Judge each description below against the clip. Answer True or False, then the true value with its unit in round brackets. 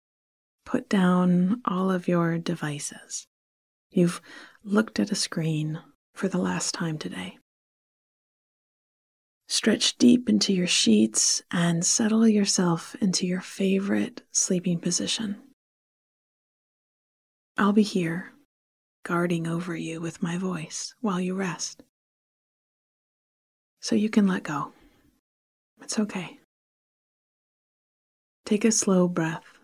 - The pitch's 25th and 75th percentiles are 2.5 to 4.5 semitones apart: True (3.8 semitones)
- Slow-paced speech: True (105 wpm)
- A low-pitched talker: False (185 Hz)